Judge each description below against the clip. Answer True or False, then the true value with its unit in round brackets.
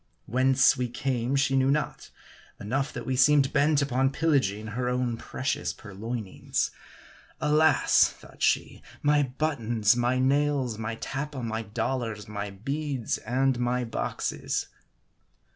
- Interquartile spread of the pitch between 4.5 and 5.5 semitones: False (3.3 semitones)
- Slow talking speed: True (125 wpm)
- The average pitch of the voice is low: True (130 Hz)